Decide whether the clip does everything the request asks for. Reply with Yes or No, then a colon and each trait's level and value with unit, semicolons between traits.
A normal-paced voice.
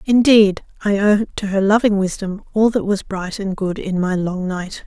No: fast, 210 wpm